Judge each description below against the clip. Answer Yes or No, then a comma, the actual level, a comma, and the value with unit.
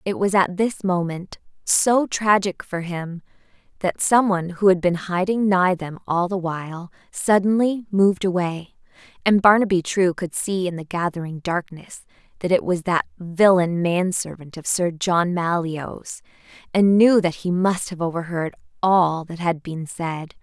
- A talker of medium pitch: Yes, medium, 180 Hz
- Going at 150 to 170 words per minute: Yes, average, 160 wpm